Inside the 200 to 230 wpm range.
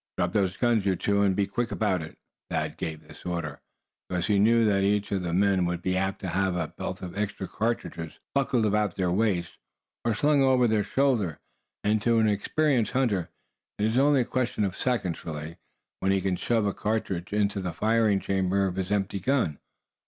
Yes: fast, 205 wpm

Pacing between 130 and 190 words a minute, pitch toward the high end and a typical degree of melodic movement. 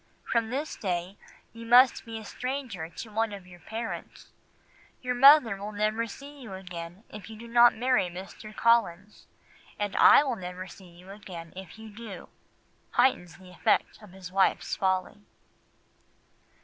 Yes: average, 160 wpm; high, 210 Hz; average, 4.0 semitones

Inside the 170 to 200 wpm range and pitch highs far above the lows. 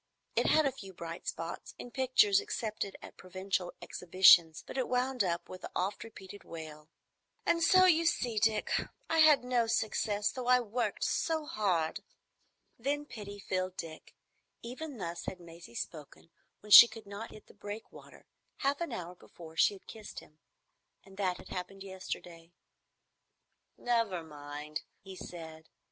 No: average, 155 wpm; wide, 6.2 semitones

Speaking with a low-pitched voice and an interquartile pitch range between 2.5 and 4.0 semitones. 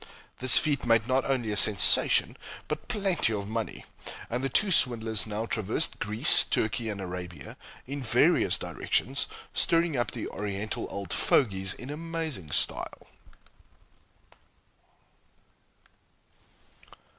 No: low, 115 Hz; average, 5.1 semitones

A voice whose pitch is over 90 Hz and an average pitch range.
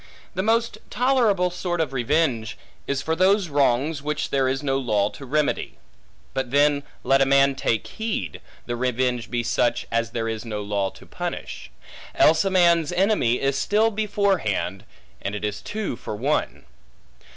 No: medium, 140 Hz; wide, 7.1 semitones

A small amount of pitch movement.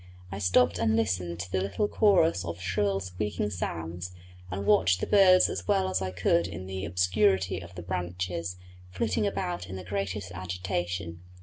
Yes: narrow, 2.0 semitones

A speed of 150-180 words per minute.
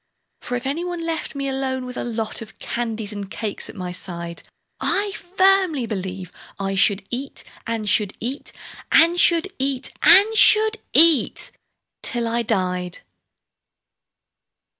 No: average, 140 wpm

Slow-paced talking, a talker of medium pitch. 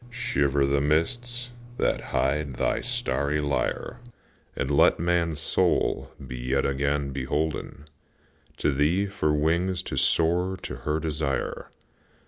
No: slow, 120 wpm; very low, 75 Hz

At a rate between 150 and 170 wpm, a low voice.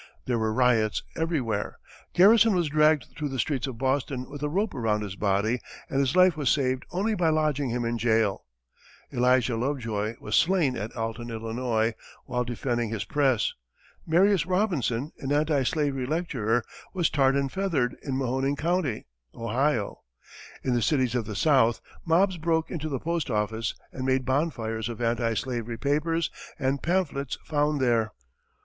Yes: average, 160 wpm; low, 130 Hz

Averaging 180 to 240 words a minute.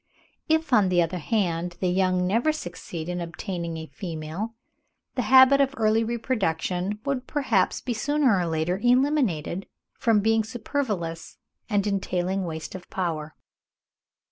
No: average, 140 wpm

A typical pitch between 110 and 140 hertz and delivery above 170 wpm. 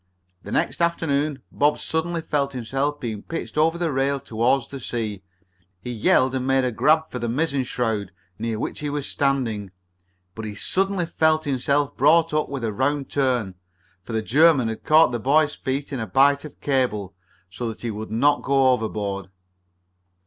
Yes: low, 135 Hz; average, 180 wpm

